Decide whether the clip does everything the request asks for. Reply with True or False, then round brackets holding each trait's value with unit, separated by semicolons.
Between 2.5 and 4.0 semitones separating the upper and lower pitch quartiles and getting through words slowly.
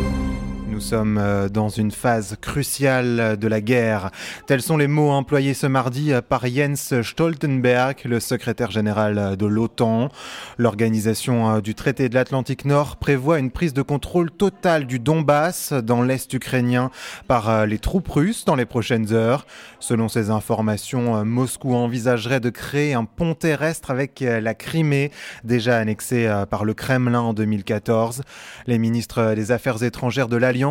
False (3.7 semitones; 150 wpm)